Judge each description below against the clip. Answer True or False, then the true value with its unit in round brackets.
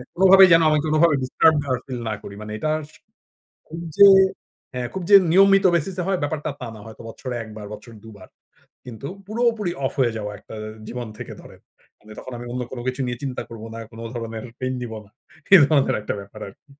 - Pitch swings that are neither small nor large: False (6.7 semitones)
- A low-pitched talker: True (130 Hz)